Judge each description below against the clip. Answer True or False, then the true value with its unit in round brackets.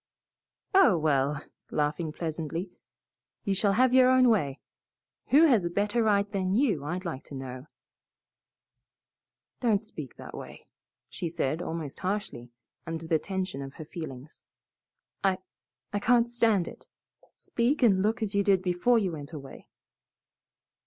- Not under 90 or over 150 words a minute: True (145 wpm)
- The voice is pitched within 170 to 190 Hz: True (185 Hz)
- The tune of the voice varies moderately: False (5.9 semitones)